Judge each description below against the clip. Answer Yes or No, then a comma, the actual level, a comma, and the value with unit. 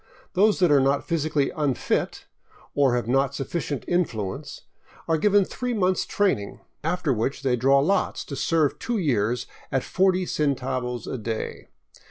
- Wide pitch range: Yes, wide, 5.9 semitones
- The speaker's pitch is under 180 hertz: Yes, medium, 140 Hz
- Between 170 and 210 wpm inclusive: No, average, 150 wpm